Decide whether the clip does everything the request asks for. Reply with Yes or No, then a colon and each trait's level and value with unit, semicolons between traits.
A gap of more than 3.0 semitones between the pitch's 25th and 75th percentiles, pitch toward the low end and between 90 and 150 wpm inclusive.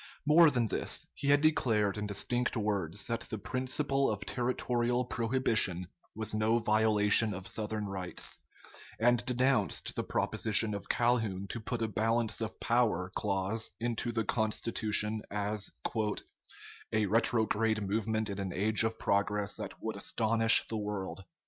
No: narrow, 2.4 semitones; low, 110 Hz; average, 140 wpm